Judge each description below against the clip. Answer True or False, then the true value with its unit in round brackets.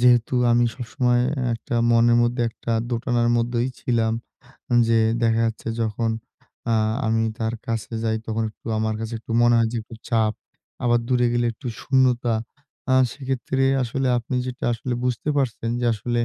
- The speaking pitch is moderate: False (120 Hz)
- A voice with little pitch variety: True (1.4 semitones)